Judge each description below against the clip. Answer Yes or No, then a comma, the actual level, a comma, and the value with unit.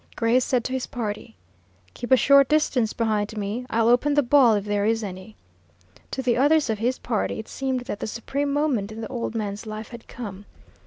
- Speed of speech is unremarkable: No, fast, 210 wpm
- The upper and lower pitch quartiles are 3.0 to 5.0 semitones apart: Yes, average, 3.4 semitones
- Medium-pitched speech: No, high, 235 Hz